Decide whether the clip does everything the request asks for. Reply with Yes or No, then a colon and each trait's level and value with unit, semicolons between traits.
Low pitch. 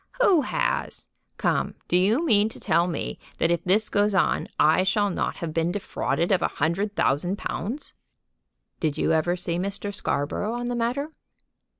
No: high, 195 Hz